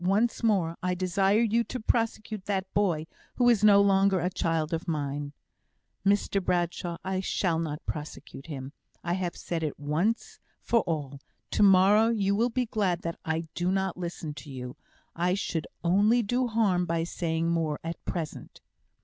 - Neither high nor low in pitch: Yes, medium, 180 Hz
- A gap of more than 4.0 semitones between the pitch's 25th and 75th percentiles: No, average, 3.7 semitones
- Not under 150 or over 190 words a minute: Yes, average, 170 wpm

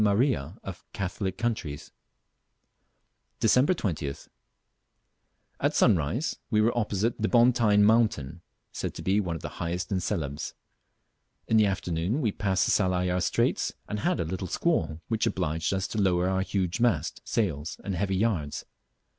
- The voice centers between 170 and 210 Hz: No, very low, 95 Hz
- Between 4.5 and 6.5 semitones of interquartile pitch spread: No, average, 4.0 semitones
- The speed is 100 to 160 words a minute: Yes, average, 150 wpm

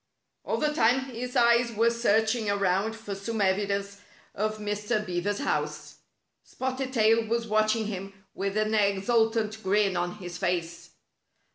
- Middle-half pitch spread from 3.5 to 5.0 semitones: No, narrow, 2.5 semitones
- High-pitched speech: Yes, high, 215 Hz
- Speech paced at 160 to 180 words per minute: No, average, 140 wpm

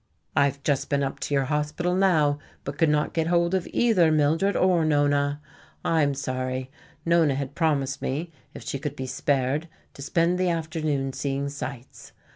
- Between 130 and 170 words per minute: No, average, 180 wpm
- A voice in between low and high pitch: Yes, medium, 145 Hz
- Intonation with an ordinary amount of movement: Yes, average, 3.0 semitones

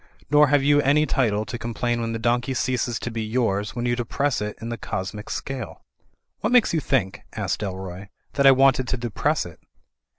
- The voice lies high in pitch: No, low, 120 Hz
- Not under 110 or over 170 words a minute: No, average, 200 wpm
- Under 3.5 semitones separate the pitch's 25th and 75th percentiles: No, average, 3.9 semitones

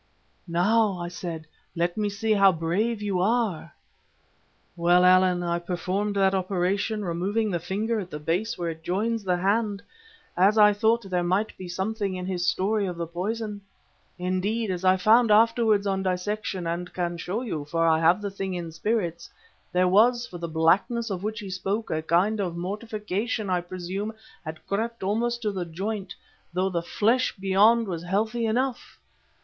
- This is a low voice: No, high, 190 Hz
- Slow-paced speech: No, average, 170 wpm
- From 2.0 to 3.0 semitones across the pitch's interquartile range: No, average, 3.4 semitones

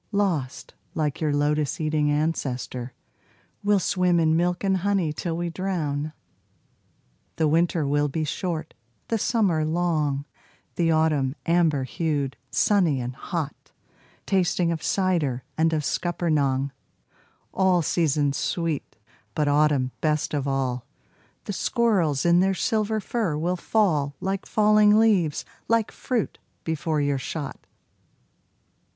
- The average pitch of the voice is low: No, medium, 160 Hz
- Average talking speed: No, slow, 125 wpm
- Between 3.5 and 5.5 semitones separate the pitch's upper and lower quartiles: Yes, average, 3.9 semitones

